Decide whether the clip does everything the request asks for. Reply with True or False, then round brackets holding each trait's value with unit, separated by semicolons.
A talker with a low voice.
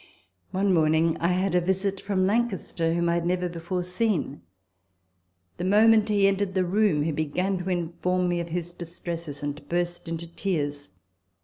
False (175 Hz)